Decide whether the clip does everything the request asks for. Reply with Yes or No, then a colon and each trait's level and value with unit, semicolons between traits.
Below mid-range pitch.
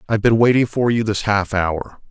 Yes: low, 105 Hz